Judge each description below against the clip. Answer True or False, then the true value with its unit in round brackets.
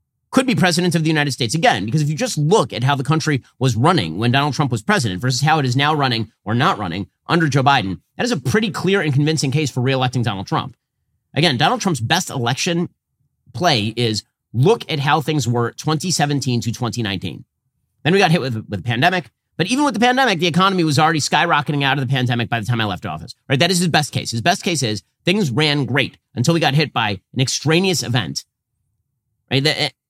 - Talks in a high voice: False (140 Hz)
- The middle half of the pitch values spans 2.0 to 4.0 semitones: False (5.2 semitones)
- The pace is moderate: False (225 wpm)